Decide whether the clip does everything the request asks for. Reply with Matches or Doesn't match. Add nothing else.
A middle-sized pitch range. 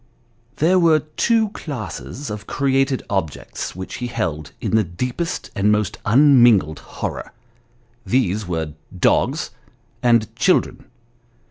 Doesn't match